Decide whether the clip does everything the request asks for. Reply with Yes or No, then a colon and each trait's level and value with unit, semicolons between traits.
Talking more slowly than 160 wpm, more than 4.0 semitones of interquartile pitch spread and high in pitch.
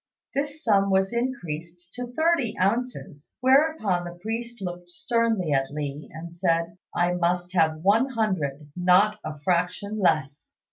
No: average, 140 wpm; wide, 5.4 semitones; medium, 180 Hz